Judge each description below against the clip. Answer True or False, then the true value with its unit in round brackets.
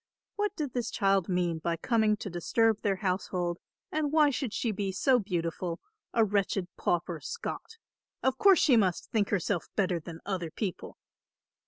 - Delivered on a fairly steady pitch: False (5.1 semitones)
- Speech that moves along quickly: False (165 wpm)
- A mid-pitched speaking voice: False (200 Hz)